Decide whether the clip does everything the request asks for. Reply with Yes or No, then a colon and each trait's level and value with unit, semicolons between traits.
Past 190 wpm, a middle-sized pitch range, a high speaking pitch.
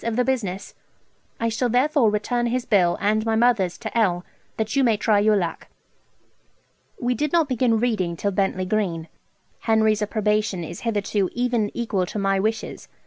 No: average, 165 wpm; average, 3.3 semitones; high, 215 Hz